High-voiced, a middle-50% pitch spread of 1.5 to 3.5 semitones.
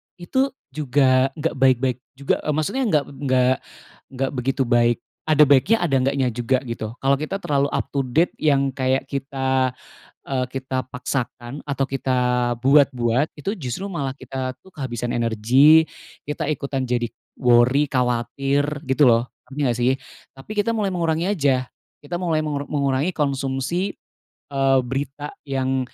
No: low, 135 Hz; narrow, 2.5 semitones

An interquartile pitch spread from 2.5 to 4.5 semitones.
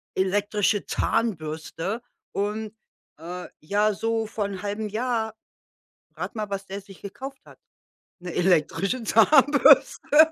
Yes: average, 2.8 semitones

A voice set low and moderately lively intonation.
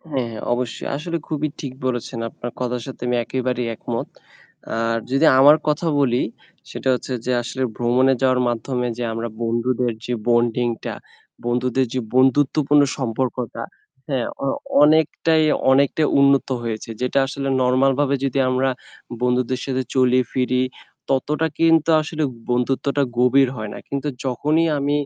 No: low, 130 Hz; narrow, 2.3 semitones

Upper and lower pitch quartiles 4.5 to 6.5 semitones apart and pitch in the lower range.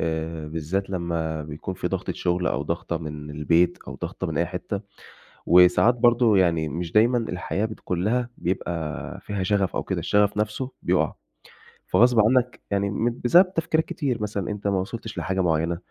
Yes: average, 5.0 semitones; very low, 95 Hz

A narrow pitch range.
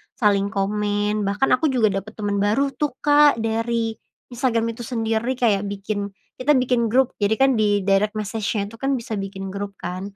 No: average, 3.2 semitones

